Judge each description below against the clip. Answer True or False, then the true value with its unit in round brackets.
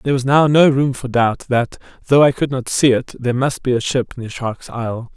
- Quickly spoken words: True (255 wpm)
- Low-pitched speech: True (130 Hz)